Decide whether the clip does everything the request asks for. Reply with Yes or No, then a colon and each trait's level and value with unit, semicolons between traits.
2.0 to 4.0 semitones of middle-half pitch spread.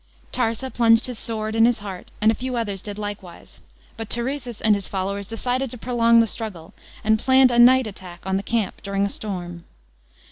Yes: average, 3.1 semitones